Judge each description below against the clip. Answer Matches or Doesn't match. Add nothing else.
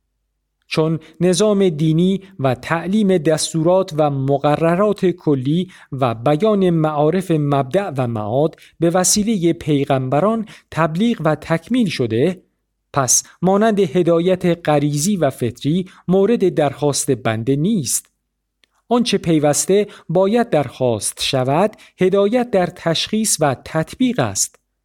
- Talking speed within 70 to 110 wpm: Matches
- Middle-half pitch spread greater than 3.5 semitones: Matches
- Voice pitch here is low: Doesn't match